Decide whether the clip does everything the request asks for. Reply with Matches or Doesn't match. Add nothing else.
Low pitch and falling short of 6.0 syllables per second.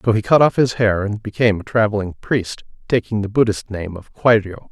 Matches